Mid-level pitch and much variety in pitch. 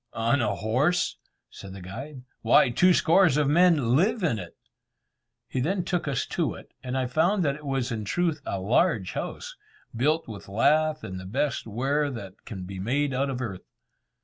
No: low, 130 Hz; wide, 5.8 semitones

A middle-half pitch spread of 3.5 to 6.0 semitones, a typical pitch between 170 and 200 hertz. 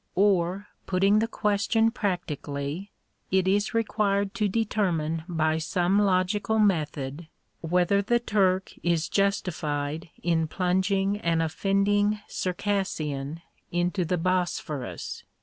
Yes: average, 3.8 semitones; medium, 185 Hz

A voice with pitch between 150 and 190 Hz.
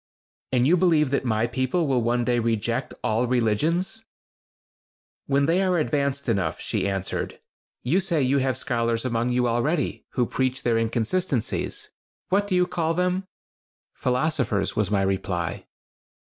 No: low, 130 Hz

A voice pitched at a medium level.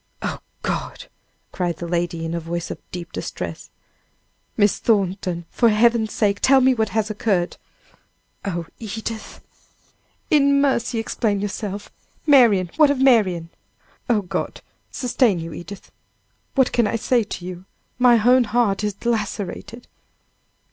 No: high, 210 Hz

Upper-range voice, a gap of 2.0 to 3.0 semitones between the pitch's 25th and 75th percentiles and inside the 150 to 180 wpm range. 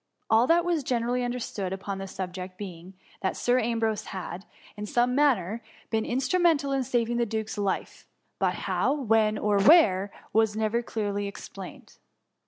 No: high, 220 Hz; average, 3.7 semitones; average, 165 wpm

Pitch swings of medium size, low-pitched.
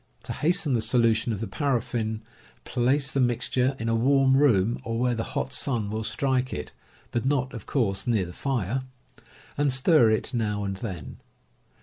Yes: average, 3.3 semitones; low, 120 Hz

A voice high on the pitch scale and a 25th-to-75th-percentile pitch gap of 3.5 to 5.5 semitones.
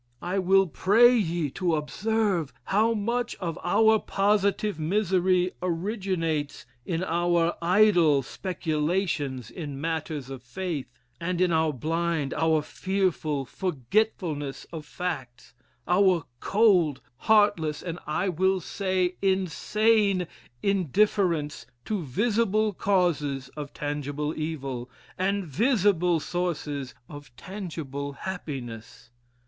No: medium, 175 Hz; average, 4.7 semitones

